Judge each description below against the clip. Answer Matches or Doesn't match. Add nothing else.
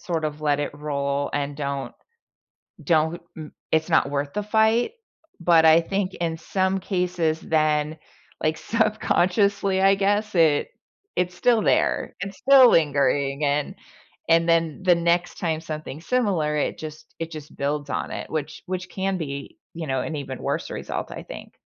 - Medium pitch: Matches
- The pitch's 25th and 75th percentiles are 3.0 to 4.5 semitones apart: Matches